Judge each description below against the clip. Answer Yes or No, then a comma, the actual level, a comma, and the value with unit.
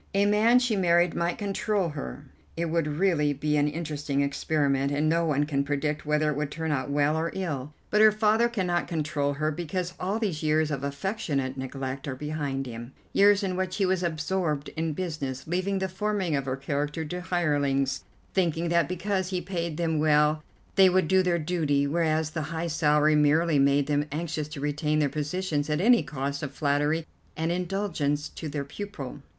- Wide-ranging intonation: No, average, 3.7 semitones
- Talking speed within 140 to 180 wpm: No, average, 190 wpm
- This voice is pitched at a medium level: Yes, medium, 155 Hz